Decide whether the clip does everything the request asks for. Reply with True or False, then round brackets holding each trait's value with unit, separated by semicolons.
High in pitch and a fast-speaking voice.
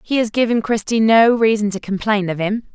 True (215 Hz; 220 wpm)